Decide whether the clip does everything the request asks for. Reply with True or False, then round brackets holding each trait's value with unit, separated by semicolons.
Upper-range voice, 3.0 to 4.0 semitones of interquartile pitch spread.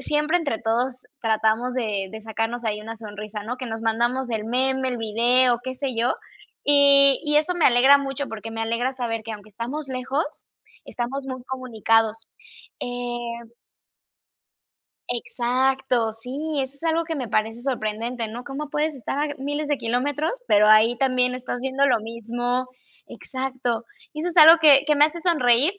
True (250 Hz; 3.5 semitones)